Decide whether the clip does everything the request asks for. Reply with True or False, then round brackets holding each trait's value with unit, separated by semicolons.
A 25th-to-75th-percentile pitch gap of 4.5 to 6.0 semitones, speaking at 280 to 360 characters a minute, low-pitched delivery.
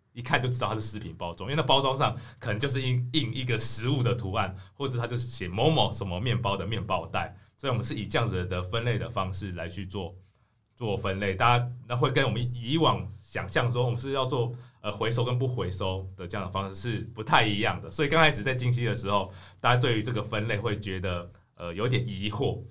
False (4.0 semitones; 345 characters per minute; 115 Hz)